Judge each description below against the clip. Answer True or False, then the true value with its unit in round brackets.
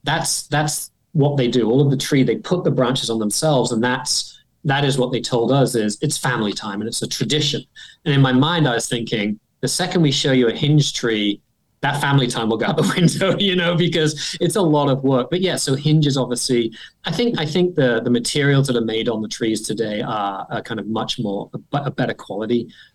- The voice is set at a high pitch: False (135 Hz)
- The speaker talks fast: True (240 wpm)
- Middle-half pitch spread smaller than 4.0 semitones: False (4.4 semitones)